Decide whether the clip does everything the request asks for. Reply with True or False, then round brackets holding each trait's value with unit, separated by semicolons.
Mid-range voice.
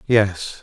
False (100 Hz)